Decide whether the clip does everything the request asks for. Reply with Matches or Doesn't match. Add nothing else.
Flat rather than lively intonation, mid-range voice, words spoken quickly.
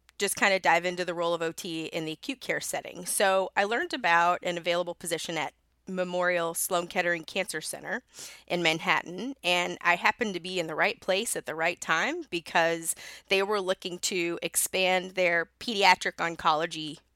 Doesn't match